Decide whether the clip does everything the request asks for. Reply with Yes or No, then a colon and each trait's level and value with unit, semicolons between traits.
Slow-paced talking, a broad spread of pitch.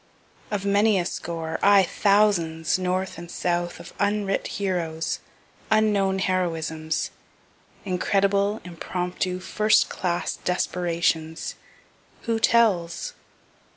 No: slow, 90 wpm; average, 2.9 semitones